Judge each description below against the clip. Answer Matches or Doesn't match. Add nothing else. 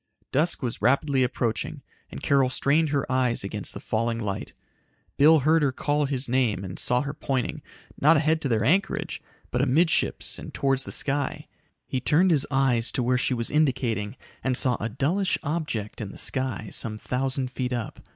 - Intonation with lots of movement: Doesn't match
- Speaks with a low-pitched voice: Matches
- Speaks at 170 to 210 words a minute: Matches